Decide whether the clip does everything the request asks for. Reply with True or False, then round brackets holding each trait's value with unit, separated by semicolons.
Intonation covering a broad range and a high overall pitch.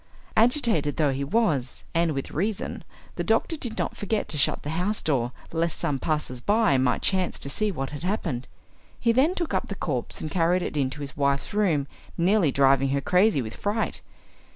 False (7.1 semitones; 165 Hz)